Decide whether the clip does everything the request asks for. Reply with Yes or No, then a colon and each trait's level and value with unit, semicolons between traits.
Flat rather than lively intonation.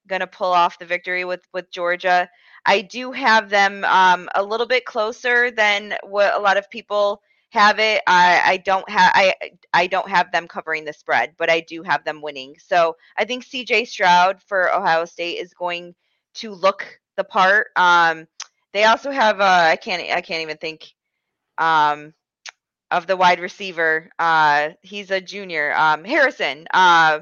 No: average, 3.8 semitones